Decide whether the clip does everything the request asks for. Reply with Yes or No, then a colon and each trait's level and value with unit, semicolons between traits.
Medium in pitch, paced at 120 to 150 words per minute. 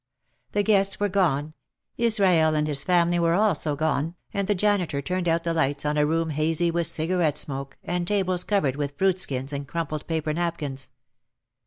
No: medium, 165 Hz; average, 180 wpm